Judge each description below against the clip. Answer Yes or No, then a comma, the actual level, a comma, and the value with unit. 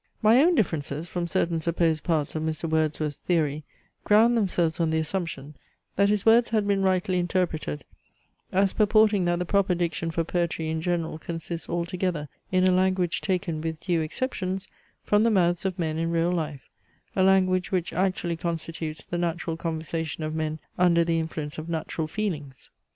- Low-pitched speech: No, medium, 170 Hz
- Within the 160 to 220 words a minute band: Yes, average, 175 wpm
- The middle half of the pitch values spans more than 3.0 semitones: No, average, 2.7 semitones